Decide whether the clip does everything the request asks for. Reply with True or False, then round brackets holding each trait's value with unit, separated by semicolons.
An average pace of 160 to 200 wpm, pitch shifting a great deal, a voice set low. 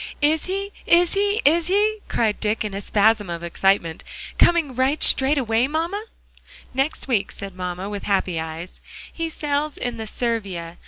False (165 wpm; 8.3 semitones; 235 Hz)